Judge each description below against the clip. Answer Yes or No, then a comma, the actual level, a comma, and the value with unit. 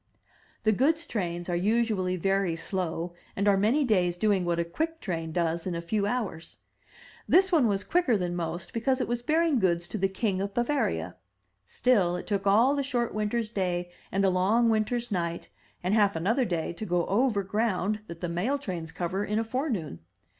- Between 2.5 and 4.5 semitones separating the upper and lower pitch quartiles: No, average, 5.1 semitones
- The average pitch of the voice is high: Yes, high, 200 Hz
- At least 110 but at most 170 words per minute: No, average, 195 wpm